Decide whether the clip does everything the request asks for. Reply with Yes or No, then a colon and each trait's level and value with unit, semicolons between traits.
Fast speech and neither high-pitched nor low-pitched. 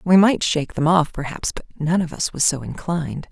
Yes: fast, 235 wpm; medium, 165 Hz